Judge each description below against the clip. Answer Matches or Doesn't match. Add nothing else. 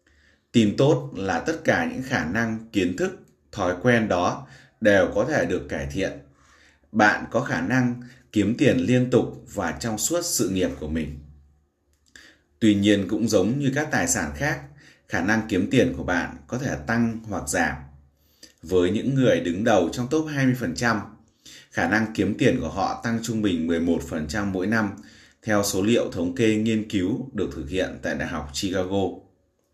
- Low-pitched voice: Matches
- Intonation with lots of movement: Matches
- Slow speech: Doesn't match